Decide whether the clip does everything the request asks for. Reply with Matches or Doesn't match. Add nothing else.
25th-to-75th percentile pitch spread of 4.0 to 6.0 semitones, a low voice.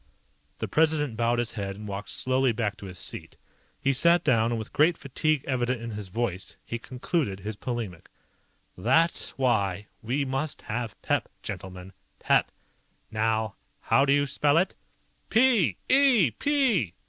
Matches